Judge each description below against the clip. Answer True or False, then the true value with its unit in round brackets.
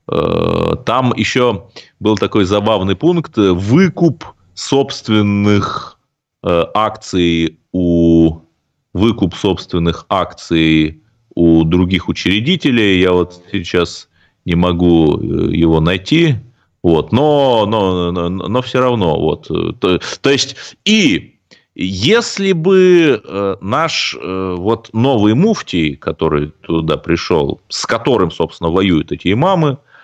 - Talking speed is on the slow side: True (100 wpm)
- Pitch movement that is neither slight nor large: False (7.5 semitones)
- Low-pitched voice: True (100 Hz)